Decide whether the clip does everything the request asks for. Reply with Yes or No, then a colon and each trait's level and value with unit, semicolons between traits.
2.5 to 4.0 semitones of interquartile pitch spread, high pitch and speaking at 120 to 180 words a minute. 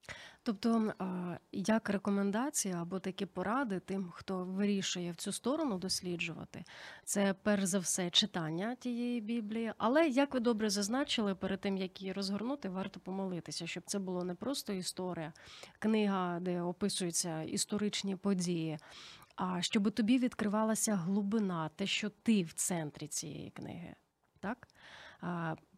Yes: average, 3.3 semitones; high, 195 Hz; average, 130 wpm